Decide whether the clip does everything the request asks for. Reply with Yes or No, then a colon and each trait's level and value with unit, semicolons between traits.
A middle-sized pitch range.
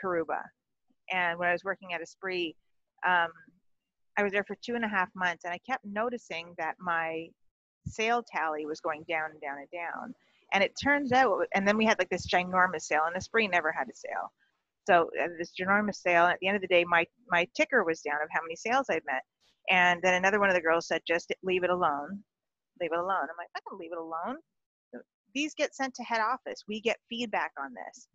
Yes: average, 4.9 semitones